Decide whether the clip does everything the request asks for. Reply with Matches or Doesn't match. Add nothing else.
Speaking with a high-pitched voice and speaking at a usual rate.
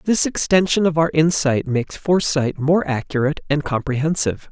Doesn't match